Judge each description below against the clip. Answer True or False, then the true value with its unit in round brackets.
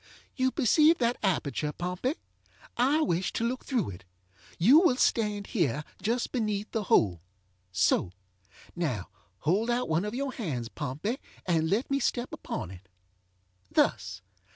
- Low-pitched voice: False (205 Hz)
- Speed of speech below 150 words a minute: True (135 wpm)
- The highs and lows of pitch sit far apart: True (8.8 semitones)